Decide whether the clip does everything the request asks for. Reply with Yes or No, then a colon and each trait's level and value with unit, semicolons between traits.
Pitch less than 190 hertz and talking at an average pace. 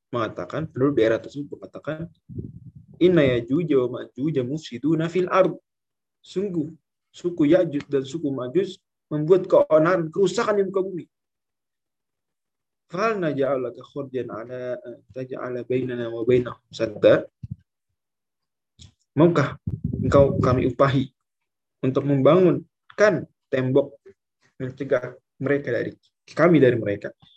Yes: medium, 140 Hz; average, 105 wpm